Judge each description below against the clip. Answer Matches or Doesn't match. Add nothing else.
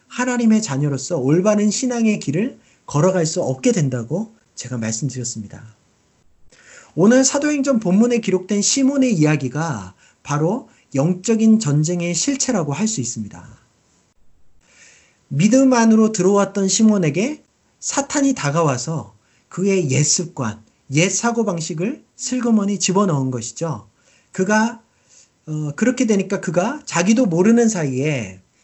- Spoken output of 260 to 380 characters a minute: Matches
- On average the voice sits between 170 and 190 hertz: Matches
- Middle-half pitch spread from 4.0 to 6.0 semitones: Doesn't match